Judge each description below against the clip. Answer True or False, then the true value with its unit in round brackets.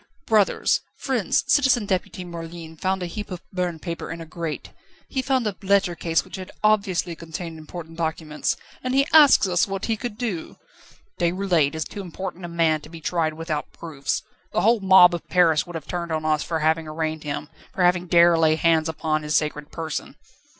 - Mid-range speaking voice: True (170 Hz)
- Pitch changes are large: False (3.1 semitones)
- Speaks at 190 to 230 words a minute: True (195 wpm)